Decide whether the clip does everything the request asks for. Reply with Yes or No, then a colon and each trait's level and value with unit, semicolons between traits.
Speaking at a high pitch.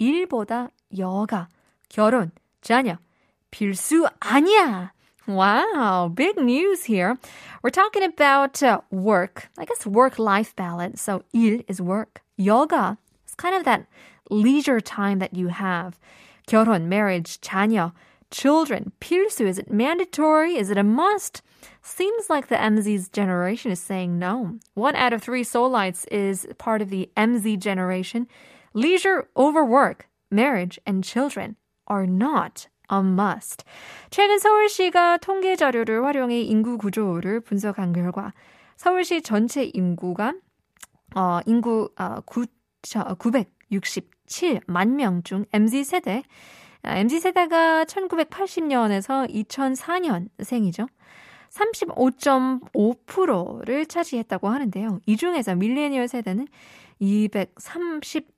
Yes: high, 230 Hz